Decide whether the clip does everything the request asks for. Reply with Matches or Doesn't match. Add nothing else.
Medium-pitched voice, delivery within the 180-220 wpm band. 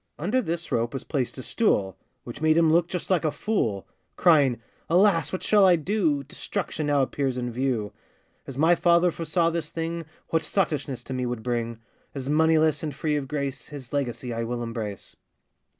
Matches